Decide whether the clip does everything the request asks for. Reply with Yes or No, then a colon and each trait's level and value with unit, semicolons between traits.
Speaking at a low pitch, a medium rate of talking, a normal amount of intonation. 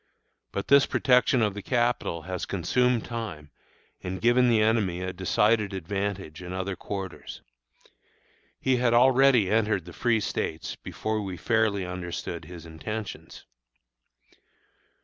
No: low, 100 Hz; slow, 130 wpm; average, 4.3 semitones